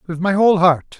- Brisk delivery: Yes, fast, 240 wpm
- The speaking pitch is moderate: Yes, medium, 180 Hz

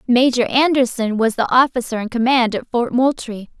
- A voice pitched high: Yes, high, 245 Hz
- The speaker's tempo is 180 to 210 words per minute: No, average, 165 wpm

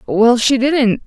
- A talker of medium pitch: No, high, 245 Hz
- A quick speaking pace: No, average, 170 wpm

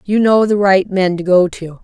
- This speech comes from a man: No, female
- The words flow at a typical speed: No, fast, 260 wpm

